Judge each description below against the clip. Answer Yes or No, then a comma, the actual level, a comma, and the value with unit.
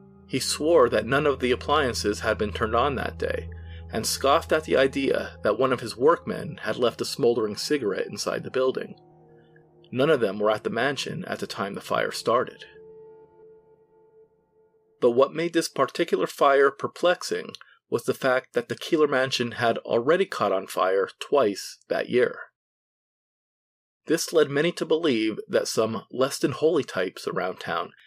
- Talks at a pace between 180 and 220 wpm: No, average, 170 wpm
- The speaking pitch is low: No, medium, 165 Hz